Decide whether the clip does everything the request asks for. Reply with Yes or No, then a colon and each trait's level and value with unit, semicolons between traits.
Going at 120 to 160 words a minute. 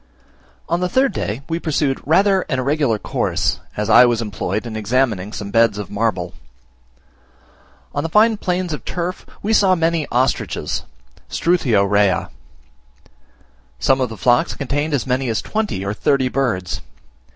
Yes: average, 150 wpm